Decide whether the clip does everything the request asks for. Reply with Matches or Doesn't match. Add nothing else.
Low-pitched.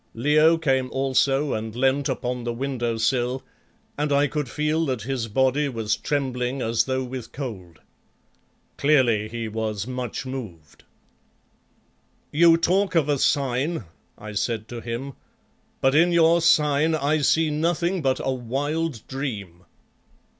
Matches